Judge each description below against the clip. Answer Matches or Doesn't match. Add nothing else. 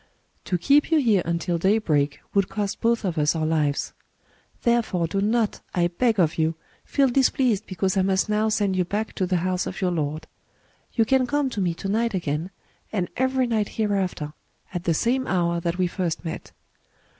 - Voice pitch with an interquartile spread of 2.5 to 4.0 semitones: Doesn't match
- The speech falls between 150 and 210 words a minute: Matches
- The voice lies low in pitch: Doesn't match